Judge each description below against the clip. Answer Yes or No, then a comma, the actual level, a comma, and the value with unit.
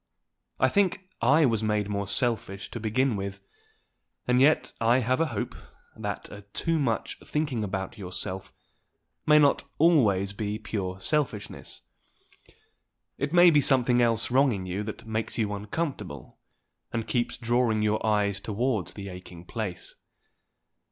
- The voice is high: No, low, 110 Hz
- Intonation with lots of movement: No, average, 4.4 semitones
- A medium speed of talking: Yes, average, 145 wpm